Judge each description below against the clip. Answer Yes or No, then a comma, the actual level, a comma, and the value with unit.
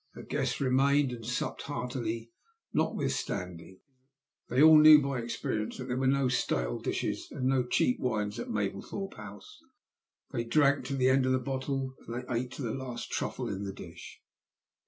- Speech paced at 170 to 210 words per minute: Yes, average, 175 wpm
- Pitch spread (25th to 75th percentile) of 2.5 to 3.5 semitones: Yes, average, 2.8 semitones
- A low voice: Yes, low, 125 Hz